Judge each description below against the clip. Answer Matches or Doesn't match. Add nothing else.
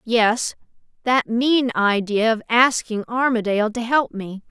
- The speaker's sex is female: Matches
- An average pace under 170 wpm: Matches